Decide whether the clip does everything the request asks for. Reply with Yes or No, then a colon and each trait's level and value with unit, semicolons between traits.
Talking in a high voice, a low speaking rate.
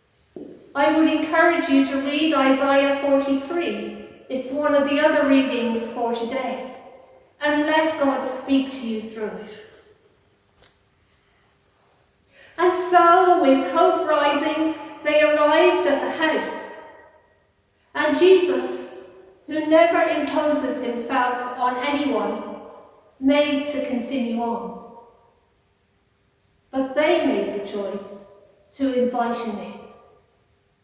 Yes: very high, 275 Hz; slow, 105 wpm